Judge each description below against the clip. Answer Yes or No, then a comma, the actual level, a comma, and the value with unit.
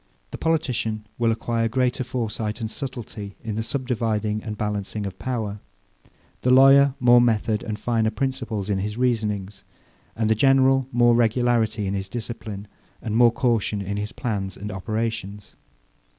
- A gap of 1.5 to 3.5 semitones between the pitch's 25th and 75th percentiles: Yes, narrow, 2.6 semitones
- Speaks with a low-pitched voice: Yes, low, 110 Hz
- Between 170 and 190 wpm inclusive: No, average, 150 wpm